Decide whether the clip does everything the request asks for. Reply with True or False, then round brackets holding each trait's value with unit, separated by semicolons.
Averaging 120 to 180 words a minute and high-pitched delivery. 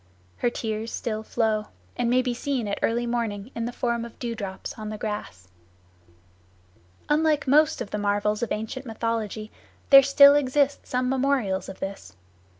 True (165 wpm; 230 Hz)